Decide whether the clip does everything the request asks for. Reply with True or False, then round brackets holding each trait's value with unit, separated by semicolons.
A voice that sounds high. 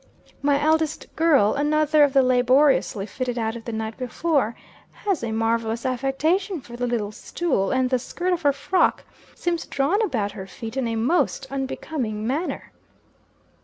True (265 Hz)